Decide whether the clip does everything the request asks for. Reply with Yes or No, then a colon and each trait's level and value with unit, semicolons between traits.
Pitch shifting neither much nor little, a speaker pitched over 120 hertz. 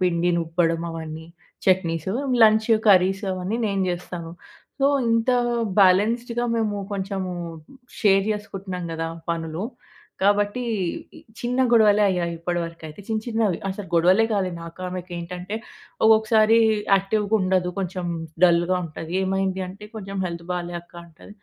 Yes: average, 3.3 semitones; high, 190 Hz